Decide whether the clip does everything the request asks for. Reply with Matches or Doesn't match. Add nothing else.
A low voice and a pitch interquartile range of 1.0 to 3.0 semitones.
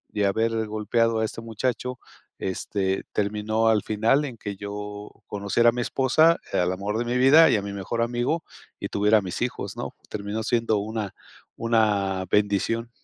Matches